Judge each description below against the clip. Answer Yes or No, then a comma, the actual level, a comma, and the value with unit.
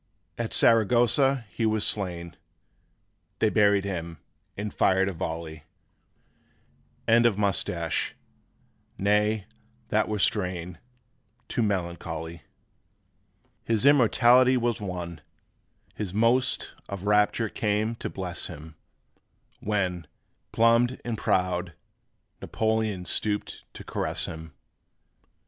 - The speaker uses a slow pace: Yes, slow, 100 wpm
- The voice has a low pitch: Yes, low, 105 Hz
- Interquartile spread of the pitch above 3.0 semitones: Yes, average, 4.1 semitones